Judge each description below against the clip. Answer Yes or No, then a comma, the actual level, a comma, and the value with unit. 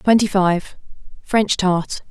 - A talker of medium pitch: No, high, 195 Hz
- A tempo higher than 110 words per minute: No, slow, 85 wpm